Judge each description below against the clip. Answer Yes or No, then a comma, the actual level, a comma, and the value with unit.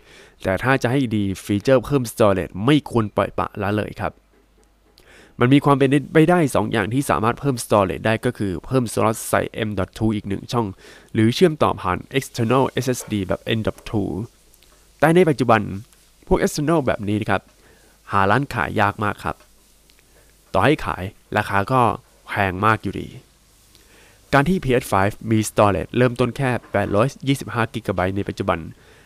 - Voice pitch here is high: No, low, 110 Hz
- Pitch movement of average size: Yes, average, 4.5 semitones